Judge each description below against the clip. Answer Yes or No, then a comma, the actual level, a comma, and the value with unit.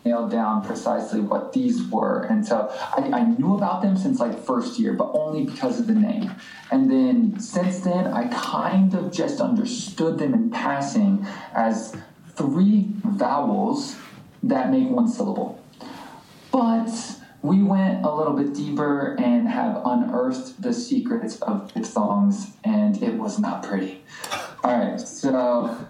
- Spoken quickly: No, average, 150 wpm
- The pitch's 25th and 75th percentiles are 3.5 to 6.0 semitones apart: Yes, average, 4.5 semitones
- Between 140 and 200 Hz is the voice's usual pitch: No, high, 220 Hz